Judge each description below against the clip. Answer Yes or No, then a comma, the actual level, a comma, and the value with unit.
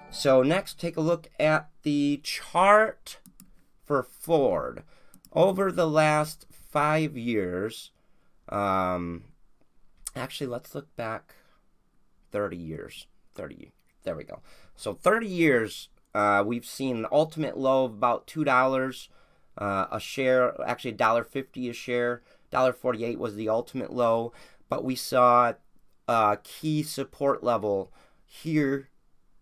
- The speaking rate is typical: No, slow, 125 wpm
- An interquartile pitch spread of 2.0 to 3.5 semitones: No, average, 4.4 semitones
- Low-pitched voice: Yes, low, 130 Hz